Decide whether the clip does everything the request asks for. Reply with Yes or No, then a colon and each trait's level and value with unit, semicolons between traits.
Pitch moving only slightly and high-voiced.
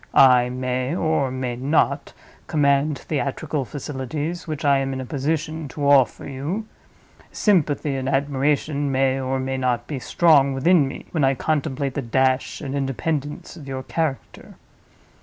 No: narrow, 2.3 semitones; medium, 140 Hz